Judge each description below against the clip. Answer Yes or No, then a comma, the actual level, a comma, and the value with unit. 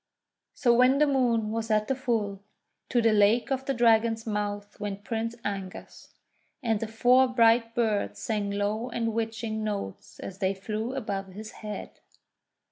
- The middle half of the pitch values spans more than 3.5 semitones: No, narrow, 2.4 semitones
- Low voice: No, high, 220 Hz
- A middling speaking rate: Yes, average, 160 wpm